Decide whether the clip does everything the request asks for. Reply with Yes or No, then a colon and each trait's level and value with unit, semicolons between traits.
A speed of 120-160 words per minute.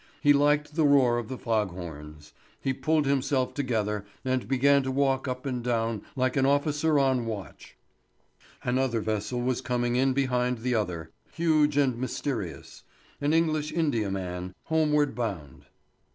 Yes: average, 150 wpm